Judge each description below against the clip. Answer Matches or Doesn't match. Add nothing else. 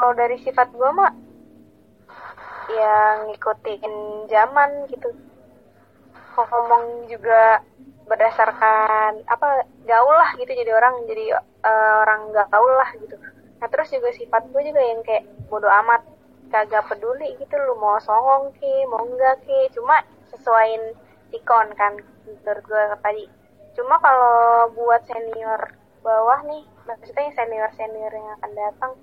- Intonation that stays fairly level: Doesn't match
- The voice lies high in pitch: Matches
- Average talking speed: Matches